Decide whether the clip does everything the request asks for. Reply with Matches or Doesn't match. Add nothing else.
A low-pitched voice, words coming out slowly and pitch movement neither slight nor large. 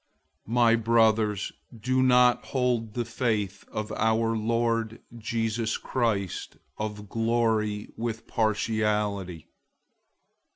Doesn't match